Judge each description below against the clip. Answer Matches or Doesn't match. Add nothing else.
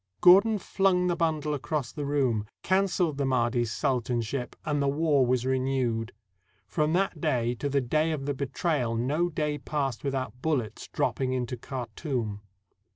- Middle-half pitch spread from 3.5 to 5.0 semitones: Matches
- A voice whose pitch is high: Doesn't match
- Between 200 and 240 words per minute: Doesn't match